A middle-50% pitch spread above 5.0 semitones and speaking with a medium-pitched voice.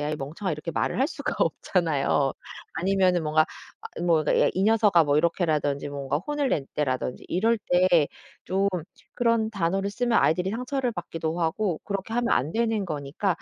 Yes: wide, 5.6 semitones; medium, 180 Hz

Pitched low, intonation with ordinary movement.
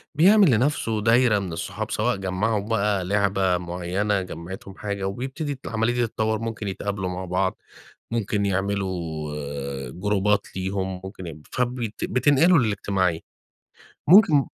Yes: low, 100 Hz; average, 3.6 semitones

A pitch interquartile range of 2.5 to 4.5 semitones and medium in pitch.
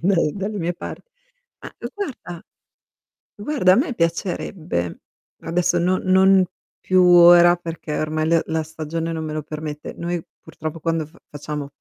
Yes: average, 2.8 semitones; medium, 170 Hz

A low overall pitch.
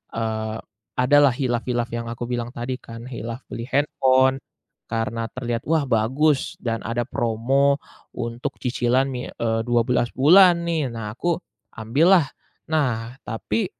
Yes: low, 120 Hz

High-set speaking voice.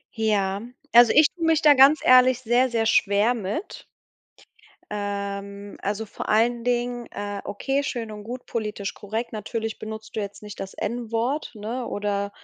Yes: high, 220 Hz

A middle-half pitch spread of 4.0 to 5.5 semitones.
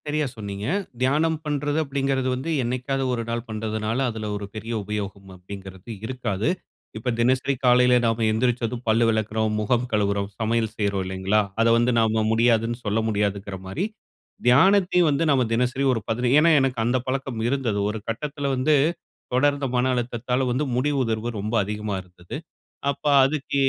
No: average, 3.6 semitones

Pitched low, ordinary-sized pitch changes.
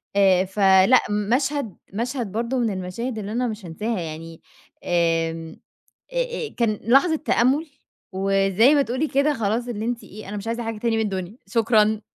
No: high, 220 Hz; average, 4.2 semitones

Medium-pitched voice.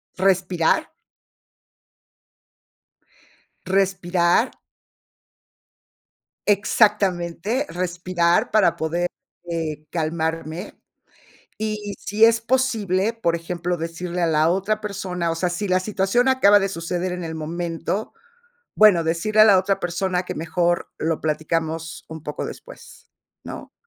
Yes: medium, 180 Hz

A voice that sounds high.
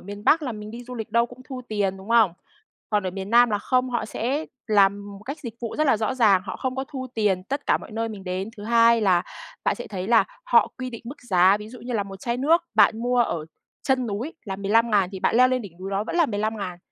Yes: high, 225 Hz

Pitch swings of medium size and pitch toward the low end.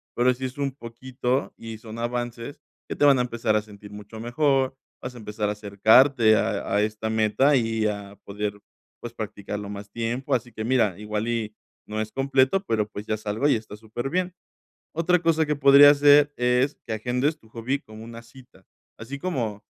Yes: average, 3.9 semitones; low, 115 Hz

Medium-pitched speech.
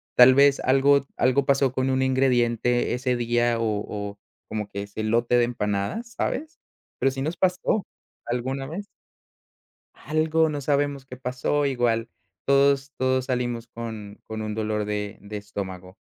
No: low, 125 Hz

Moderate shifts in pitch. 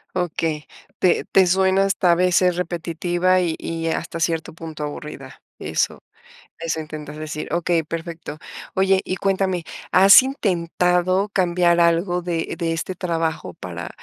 No: narrow, 2.1 semitones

